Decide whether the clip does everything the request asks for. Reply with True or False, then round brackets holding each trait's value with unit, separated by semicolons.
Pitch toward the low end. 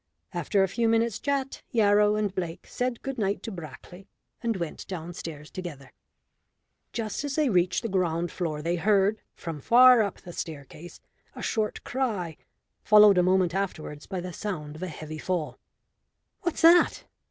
False (190 Hz)